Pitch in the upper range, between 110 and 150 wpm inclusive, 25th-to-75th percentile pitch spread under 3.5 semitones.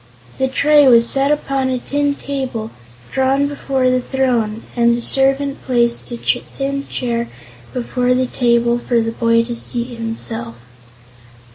Yes: very high, 250 Hz; average, 145 wpm; narrow, 2.4 semitones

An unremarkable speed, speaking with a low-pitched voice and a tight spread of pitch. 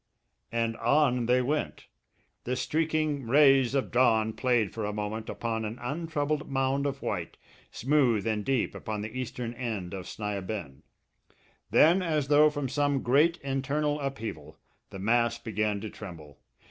No: average, 155 wpm; low, 125 Hz; average, 4.6 semitones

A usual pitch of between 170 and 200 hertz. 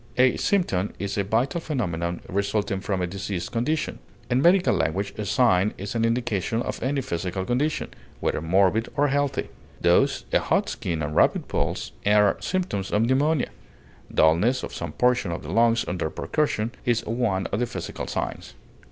No: low, 110 Hz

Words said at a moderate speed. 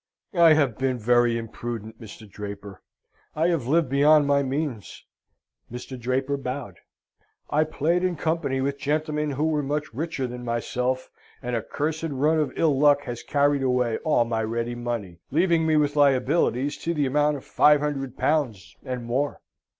Yes: average, 165 wpm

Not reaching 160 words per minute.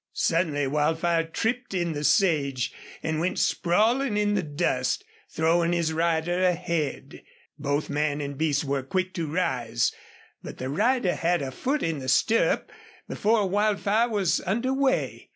Yes: average, 150 wpm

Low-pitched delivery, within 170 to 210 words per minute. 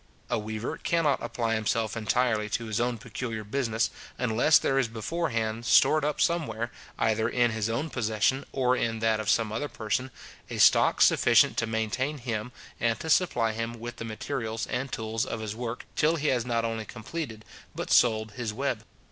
Yes: low, 115 Hz; average, 180 wpm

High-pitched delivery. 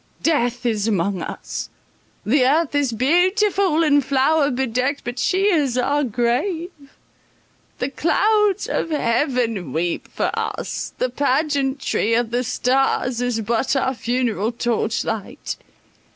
Yes: very high, 255 Hz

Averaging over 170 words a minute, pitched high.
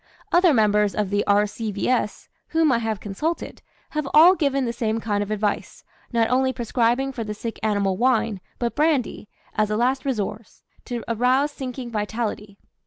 No: average, 165 wpm; high, 230 Hz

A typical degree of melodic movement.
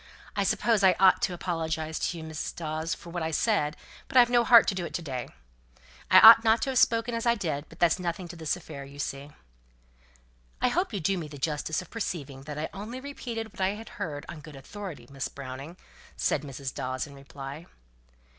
No: wide, 6.4 semitones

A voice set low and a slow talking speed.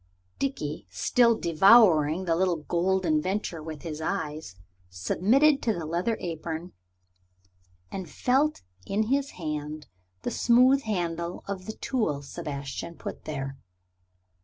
No: medium, 170 Hz; slow, 120 wpm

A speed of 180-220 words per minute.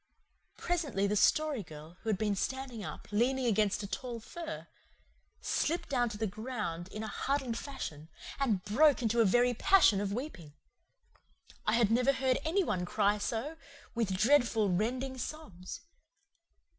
No: average, 155 wpm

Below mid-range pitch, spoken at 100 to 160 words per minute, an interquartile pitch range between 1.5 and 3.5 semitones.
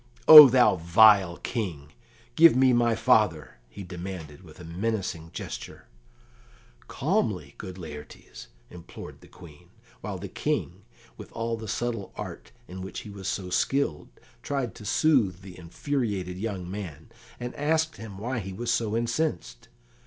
No: low, 100 Hz; average, 145 wpm; average, 5.0 semitones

